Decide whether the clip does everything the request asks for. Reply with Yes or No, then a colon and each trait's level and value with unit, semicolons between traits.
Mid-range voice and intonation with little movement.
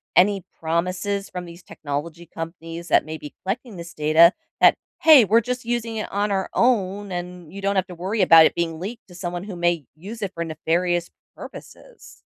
No: medium, 180 Hz; average, 3.3 semitones